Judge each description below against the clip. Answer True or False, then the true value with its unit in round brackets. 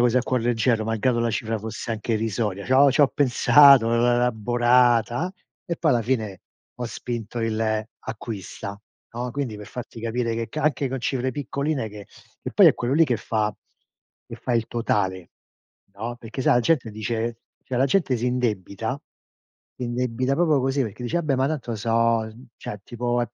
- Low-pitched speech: True (120 Hz)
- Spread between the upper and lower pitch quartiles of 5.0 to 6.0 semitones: False (2.6 semitones)